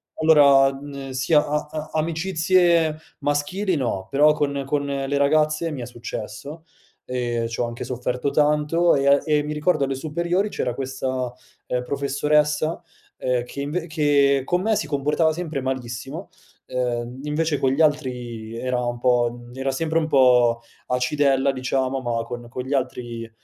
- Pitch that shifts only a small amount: No, average, 3.4 semitones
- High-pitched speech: No, medium, 140 Hz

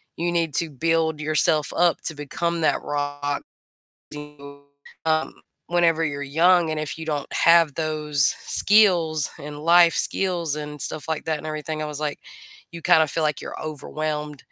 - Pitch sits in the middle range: Yes, medium, 155 Hz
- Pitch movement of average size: No, narrow, 2.0 semitones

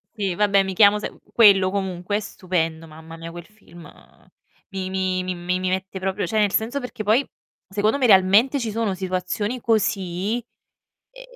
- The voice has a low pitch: No, high, 195 Hz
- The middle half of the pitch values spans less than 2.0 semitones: No, average, 2.7 semitones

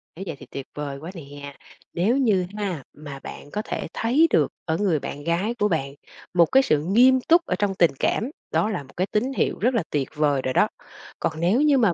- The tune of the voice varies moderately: No, wide, 7.4 semitones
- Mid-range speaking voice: Yes, medium, 180 Hz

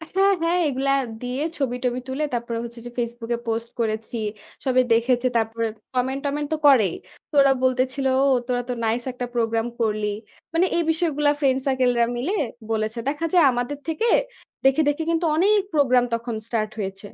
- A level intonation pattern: No, average, 3.7 semitones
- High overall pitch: Yes, very high, 250 Hz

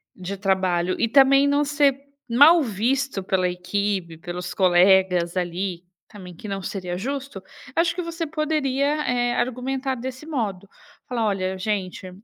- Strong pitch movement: Yes, wide, 6.8 semitones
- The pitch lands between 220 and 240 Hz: No, high, 210 Hz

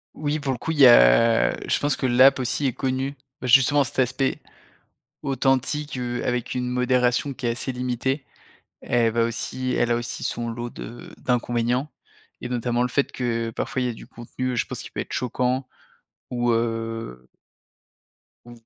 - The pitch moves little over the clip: Yes, narrow, 1.9 semitones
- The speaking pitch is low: Yes, low, 125 Hz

